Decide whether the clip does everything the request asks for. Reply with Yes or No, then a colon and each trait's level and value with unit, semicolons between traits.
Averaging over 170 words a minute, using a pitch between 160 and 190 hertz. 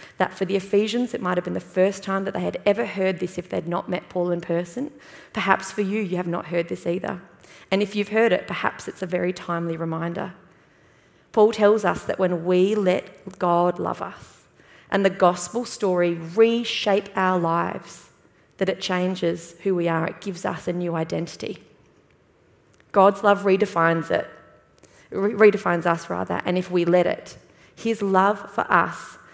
Yes: average, 185 wpm; medium, 185 Hz